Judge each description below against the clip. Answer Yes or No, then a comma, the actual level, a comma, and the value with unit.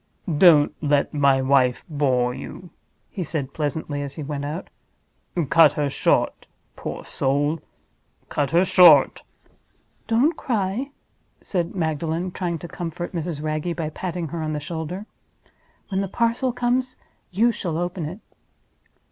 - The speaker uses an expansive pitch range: No, average, 4.0 semitones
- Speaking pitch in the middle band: Yes, medium, 165 Hz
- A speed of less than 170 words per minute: Yes, average, 140 wpm